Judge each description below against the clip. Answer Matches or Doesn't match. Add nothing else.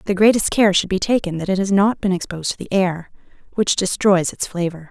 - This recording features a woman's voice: Matches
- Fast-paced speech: Matches